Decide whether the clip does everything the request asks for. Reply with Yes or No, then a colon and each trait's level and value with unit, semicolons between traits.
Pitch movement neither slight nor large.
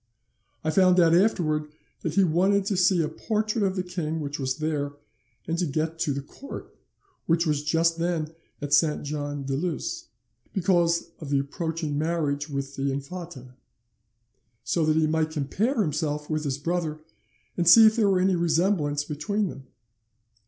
Yes: average, 3.4 semitones